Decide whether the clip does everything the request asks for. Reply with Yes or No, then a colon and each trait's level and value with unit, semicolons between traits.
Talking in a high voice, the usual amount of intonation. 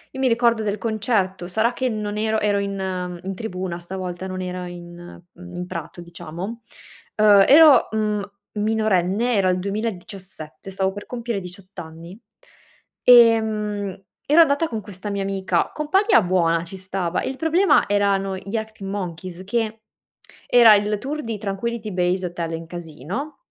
Yes: high, 200 Hz; average, 3.5 semitones